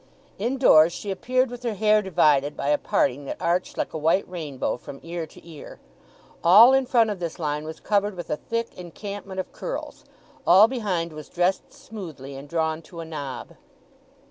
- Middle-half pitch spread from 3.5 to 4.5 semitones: No, average, 5.3 semitones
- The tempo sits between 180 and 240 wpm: Yes, average, 185 wpm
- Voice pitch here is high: No, medium, 175 Hz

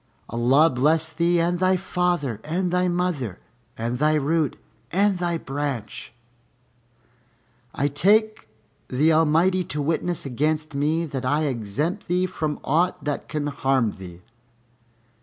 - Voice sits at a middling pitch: Yes, medium, 155 Hz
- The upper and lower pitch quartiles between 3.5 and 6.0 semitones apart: Yes, average, 4.4 semitones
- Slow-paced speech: Yes, slow, 130 wpm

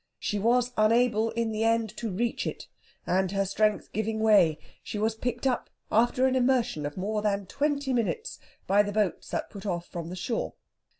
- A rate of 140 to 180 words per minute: No, average, 190 wpm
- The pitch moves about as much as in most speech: Yes, average, 3.2 semitones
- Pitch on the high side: Yes, high, 220 Hz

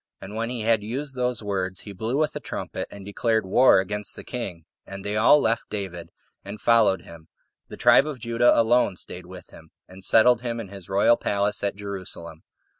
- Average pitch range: Yes, average, 3.5 semitones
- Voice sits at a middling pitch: No, low, 105 Hz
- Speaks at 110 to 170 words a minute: No, average, 200 wpm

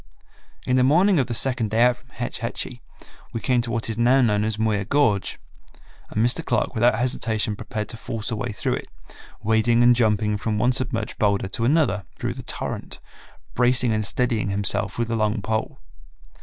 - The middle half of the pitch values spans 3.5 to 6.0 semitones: No, narrow, 2.4 semitones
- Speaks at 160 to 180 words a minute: No, average, 195 wpm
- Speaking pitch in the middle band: No, low, 115 Hz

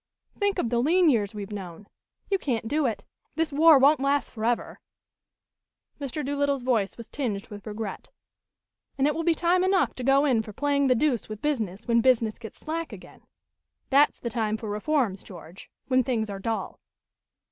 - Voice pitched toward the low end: No, very high, 250 Hz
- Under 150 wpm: No, average, 185 wpm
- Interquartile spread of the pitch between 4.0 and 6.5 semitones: Yes, average, 5.2 semitones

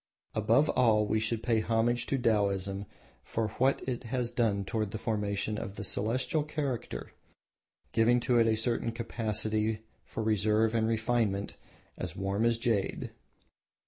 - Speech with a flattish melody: Yes, narrow, 2.0 semitones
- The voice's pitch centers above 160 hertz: No, low, 110 Hz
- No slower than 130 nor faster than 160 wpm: Yes, average, 145 wpm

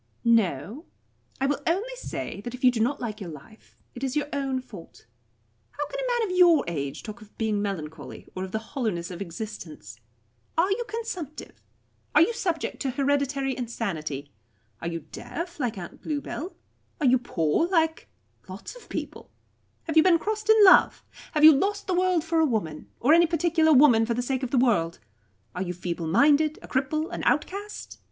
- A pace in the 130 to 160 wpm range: No, average, 190 wpm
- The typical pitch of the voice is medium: No, very high, 270 Hz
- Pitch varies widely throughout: Yes, wide, 8.3 semitones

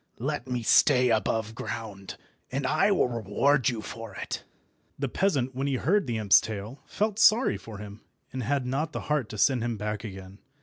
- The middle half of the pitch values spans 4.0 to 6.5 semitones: Yes, average, 4.6 semitones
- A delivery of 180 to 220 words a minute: Yes, average, 185 wpm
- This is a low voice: Yes, low, 125 Hz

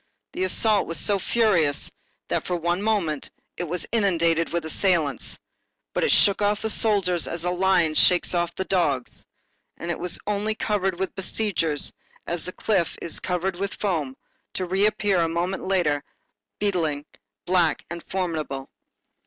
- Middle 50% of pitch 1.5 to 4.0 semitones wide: Yes, average, 3.1 semitones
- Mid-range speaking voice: Yes, medium, 180 Hz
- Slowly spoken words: No, average, 155 wpm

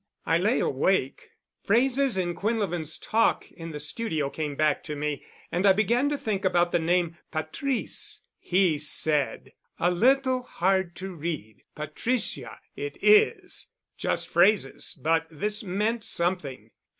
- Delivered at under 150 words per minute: Yes, slow, 135 wpm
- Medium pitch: Yes, medium, 180 Hz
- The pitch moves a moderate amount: No, wide, 6.0 semitones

